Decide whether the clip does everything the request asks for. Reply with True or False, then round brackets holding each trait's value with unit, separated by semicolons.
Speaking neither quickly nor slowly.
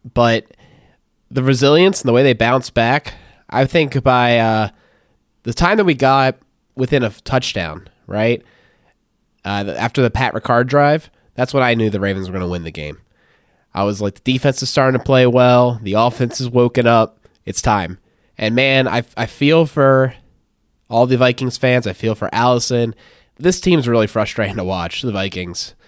True (185 wpm)